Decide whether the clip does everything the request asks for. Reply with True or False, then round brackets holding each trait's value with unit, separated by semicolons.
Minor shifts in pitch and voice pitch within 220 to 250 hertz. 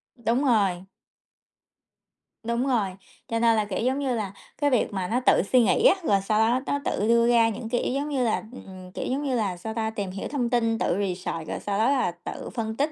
False (3.8 semitones; 230 Hz)